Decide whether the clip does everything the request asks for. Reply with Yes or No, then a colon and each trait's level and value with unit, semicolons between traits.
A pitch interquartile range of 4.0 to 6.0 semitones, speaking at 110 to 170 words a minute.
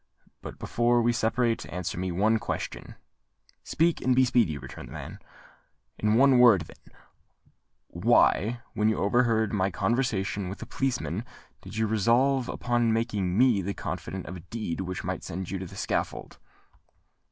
Yes: average, 4.3 semitones; average, 155 wpm